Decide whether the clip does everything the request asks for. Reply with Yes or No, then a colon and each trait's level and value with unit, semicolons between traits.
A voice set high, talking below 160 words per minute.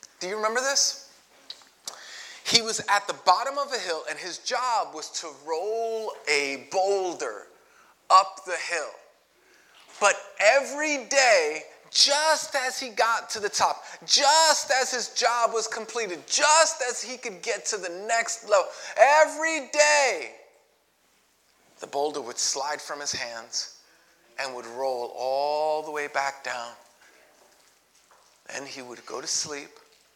Yes: high, 235 Hz; average, 140 wpm